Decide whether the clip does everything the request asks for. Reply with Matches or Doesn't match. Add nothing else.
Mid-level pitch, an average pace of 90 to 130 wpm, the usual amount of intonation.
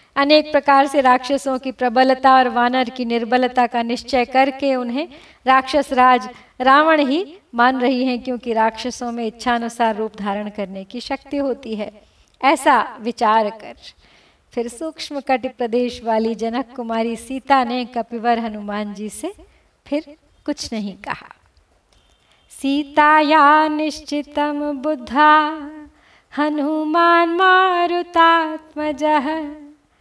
Doesn't match